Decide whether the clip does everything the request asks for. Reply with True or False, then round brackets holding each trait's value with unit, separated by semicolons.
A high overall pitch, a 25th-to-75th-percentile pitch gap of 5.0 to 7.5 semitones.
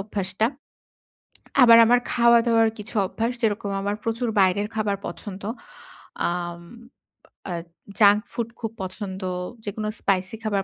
False (210 Hz; 2.9 semitones)